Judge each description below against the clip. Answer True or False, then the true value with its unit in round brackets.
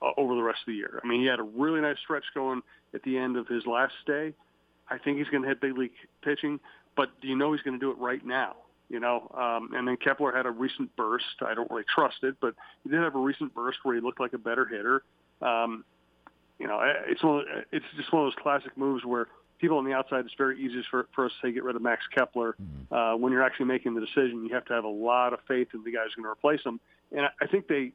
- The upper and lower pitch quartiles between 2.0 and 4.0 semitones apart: True (2.9 semitones)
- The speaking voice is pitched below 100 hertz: False (130 Hz)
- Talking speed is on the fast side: True (275 wpm)